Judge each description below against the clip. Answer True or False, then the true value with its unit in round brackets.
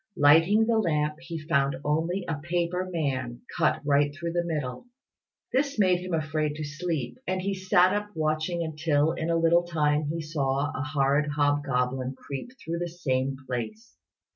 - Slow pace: False (165 wpm)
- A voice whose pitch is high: False (155 Hz)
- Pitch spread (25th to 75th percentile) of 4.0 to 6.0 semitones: False (3.2 semitones)